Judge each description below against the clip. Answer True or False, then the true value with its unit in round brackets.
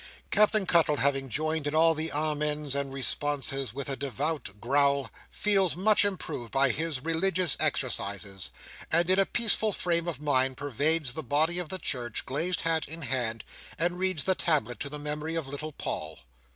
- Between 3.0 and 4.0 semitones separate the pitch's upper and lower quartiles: True (3.5 semitones)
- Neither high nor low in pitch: True (150 Hz)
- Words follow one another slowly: False (175 wpm)